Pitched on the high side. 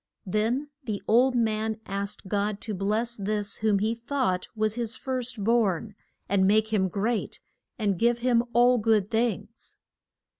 Yes: high, 220 Hz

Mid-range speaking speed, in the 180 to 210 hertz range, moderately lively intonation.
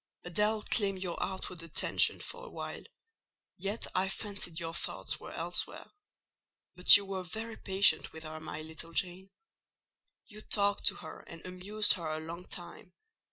Yes: average, 160 wpm; medium, 185 Hz; average, 3.4 semitones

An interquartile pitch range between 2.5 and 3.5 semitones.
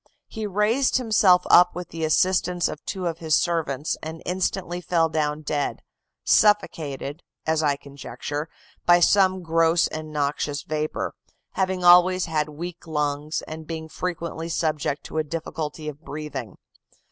Yes: average, 2.9 semitones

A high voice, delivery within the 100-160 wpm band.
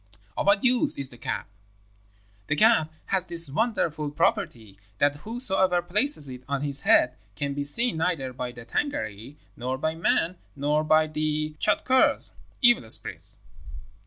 No: medium, 155 Hz; average, 150 wpm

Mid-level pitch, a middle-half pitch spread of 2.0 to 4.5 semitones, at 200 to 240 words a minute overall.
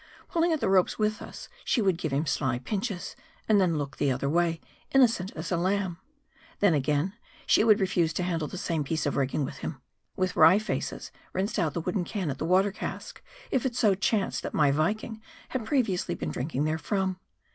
No: medium, 180 Hz; average, 5.0 semitones; fast, 205 wpm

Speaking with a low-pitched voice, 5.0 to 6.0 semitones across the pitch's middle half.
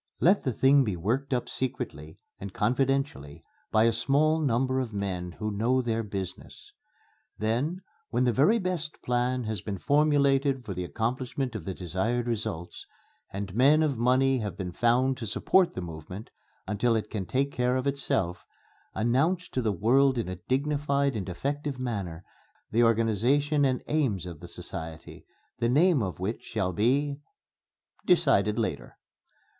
Yes: low, 120 Hz; wide, 5.5 semitones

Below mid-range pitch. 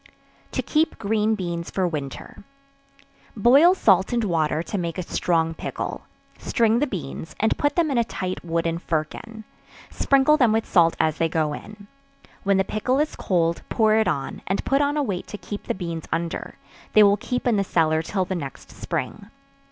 No: high, 195 Hz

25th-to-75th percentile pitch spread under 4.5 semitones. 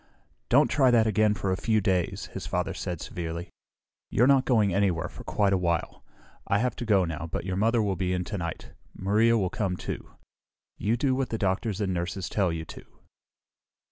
Yes: average, 3.9 semitones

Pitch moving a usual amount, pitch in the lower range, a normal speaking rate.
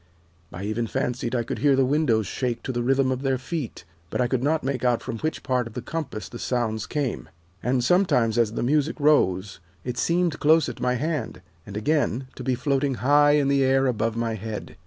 No: average, 3.6 semitones; low, 130 Hz; fast, 220 wpm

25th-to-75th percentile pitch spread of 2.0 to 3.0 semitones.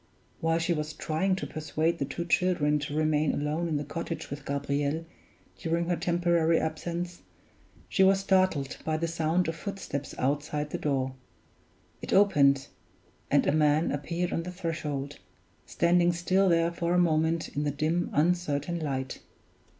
Yes: average, 2.7 semitones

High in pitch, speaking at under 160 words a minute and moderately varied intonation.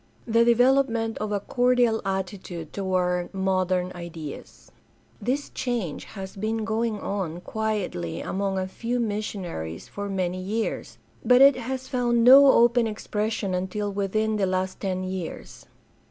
Yes: high, 205 Hz; average, 140 wpm; average, 3.8 semitones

